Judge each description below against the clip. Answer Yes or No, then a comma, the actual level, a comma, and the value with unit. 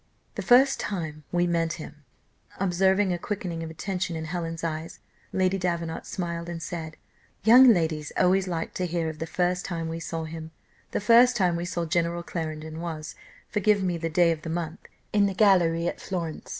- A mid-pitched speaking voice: Yes, medium, 170 Hz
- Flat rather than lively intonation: Yes, narrow, 2.3 semitones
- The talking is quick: No, average, 190 wpm